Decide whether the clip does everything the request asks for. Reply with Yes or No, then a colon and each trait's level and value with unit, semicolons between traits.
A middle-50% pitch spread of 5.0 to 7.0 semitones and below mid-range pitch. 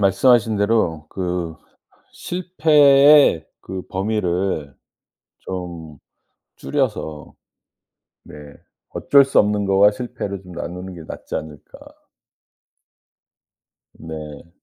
Yes: average, 5.3 semitones; very low, 95 Hz